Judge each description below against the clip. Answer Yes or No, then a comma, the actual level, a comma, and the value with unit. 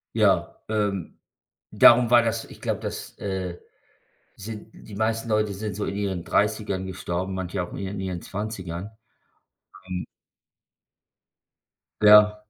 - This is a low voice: Yes, low, 100 Hz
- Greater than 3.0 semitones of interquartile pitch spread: No, narrow, 2.4 semitones